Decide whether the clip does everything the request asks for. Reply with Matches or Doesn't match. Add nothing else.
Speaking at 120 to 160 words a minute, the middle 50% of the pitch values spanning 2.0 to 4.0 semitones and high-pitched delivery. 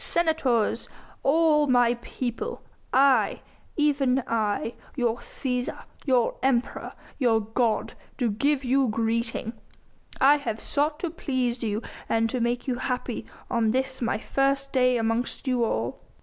Matches